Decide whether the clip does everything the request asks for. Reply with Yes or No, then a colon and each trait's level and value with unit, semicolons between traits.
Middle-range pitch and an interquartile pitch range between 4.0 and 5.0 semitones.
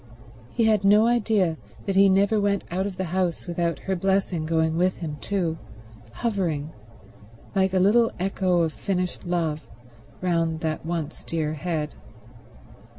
No: medium, 180 Hz; average, 3.2 semitones